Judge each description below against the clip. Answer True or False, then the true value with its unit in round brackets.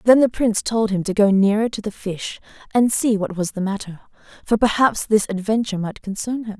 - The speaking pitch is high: True (210 Hz)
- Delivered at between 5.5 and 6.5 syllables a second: True (5.6 syllables/s)